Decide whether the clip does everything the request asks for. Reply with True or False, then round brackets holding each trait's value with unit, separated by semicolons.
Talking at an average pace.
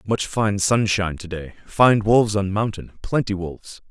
True (155 wpm)